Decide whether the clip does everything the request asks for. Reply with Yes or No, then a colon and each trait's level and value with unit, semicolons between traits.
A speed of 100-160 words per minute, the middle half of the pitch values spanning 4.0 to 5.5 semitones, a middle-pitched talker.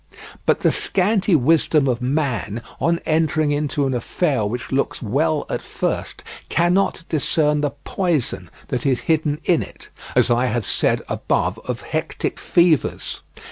Yes: average, 145 wpm; average, 4.4 semitones; medium, 150 Hz